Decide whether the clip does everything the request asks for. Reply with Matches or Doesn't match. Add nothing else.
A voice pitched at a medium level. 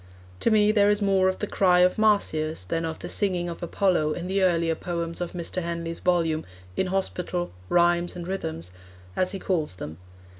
Matches